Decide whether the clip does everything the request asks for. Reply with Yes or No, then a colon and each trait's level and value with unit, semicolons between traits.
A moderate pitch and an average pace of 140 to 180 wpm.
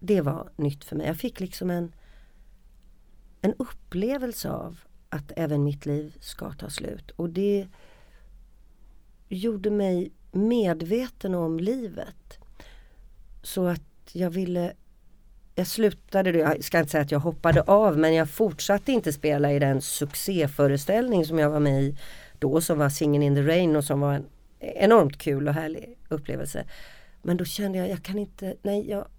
Yes: medium, 165 Hz; average, 160 wpm